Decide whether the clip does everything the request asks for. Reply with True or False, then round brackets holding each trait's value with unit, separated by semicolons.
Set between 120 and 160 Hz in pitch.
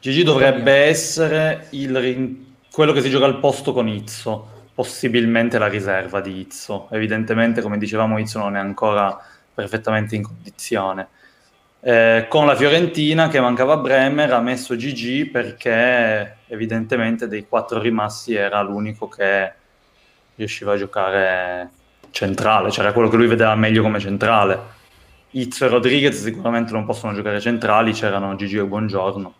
False (110 Hz)